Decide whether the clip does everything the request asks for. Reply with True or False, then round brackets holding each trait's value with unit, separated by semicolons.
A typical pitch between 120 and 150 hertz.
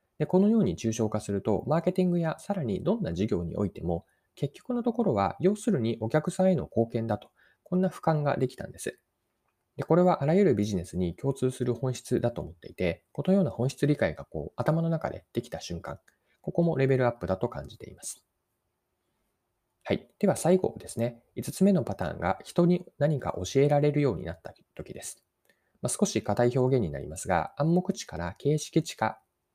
True (140 Hz)